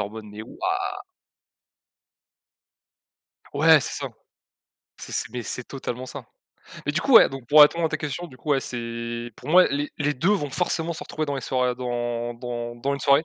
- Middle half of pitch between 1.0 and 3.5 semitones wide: No, average, 3.9 semitones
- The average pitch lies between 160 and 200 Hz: No, low, 135 Hz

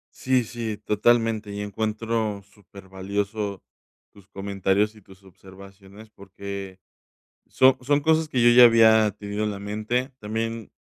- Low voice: Yes, low, 105 Hz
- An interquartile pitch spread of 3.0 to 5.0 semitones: No, narrow, 2.4 semitones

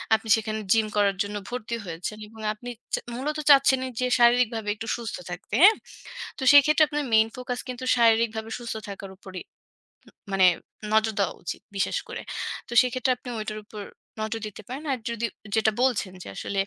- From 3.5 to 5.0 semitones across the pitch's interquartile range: No, average, 2.9 semitones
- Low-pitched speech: No, high, 225 Hz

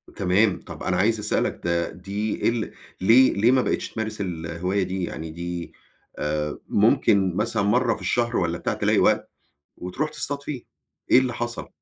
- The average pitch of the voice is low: Yes, low, 100 Hz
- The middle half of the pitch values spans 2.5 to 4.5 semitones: No, average, 5.1 semitones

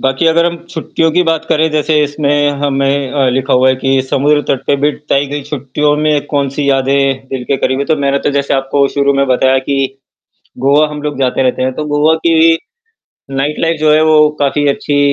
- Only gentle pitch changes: Yes, narrow, 1.9 semitones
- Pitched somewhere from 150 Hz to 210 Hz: No, medium, 140 Hz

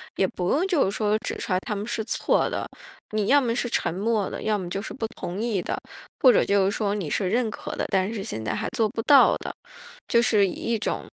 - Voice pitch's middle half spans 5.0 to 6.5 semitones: No, average, 3.0 semitones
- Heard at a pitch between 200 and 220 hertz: Yes, high, 210 Hz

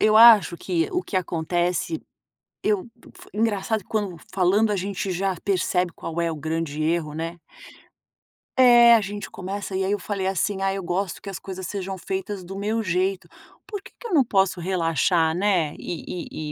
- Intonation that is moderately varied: Yes, average, 3.0 semitones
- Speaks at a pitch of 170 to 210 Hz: Yes, high, 190 Hz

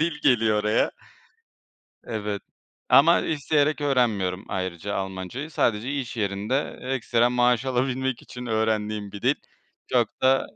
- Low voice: Yes, low, 120 Hz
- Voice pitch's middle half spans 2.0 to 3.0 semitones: No, average, 4.0 semitones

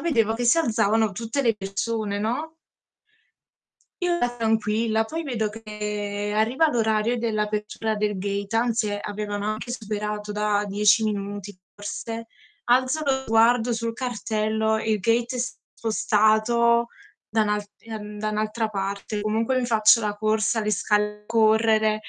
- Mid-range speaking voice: No, high, 220 Hz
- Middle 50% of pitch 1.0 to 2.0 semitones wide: Yes, narrow, 1.7 semitones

